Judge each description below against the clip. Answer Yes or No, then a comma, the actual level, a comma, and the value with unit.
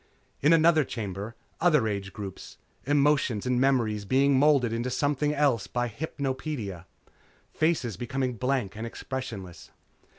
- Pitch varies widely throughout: No, average, 4.7 semitones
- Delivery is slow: Yes, slow, 125 wpm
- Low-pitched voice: Yes, low, 125 Hz